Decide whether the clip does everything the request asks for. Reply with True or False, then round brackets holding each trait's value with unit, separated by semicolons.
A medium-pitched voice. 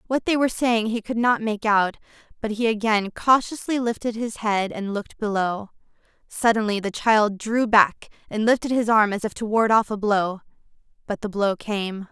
False (215 Hz)